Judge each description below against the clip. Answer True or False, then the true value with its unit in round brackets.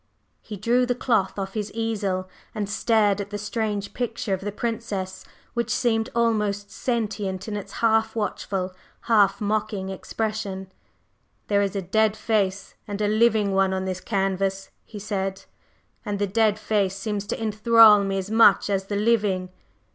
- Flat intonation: True (2.3 semitones)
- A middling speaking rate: True (160 wpm)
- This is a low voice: False (205 Hz)